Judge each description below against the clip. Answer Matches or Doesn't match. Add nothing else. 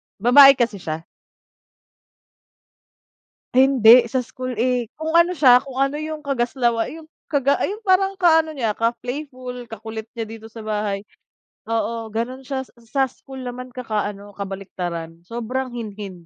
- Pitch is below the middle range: Doesn't match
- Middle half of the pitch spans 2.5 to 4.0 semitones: Matches